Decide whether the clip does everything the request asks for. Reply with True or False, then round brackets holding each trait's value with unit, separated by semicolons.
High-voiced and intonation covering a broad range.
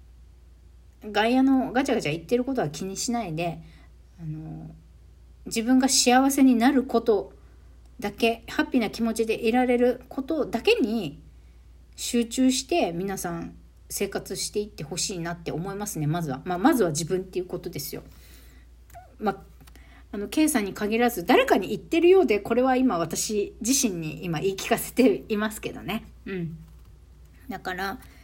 True (200 Hz; 8.5 semitones)